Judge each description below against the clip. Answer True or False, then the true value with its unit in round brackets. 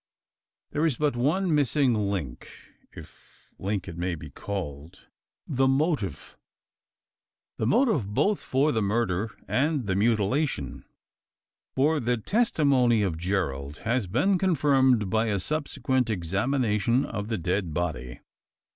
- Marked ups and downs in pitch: True (6.7 semitones)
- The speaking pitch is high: False (115 Hz)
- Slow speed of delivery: True (125 wpm)